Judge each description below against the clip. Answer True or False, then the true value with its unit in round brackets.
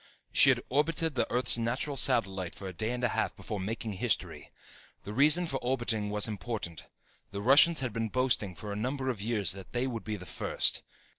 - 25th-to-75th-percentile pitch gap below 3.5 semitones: False (4.2 semitones)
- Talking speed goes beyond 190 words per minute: True (200 wpm)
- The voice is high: False (115 Hz)